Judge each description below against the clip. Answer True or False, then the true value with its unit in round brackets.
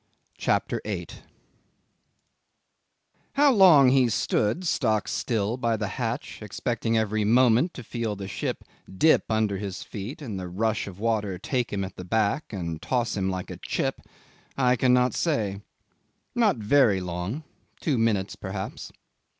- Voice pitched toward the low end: True (110 Hz)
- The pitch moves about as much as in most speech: True (4.2 semitones)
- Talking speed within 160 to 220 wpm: False (145 wpm)